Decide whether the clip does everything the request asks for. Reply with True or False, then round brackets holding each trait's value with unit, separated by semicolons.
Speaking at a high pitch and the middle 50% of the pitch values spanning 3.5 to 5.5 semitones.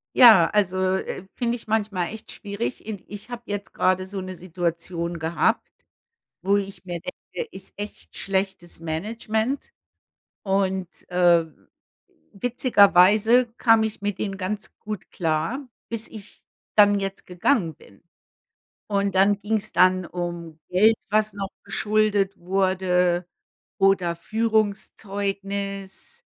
False (195 Hz; 2.8 semitones)